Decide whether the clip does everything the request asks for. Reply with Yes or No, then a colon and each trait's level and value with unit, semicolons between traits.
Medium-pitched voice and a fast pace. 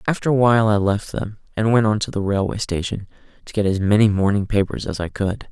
No: low, 105 Hz; fast, 240 wpm